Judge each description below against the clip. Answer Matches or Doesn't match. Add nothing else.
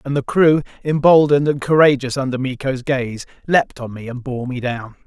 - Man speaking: Matches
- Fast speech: Doesn't match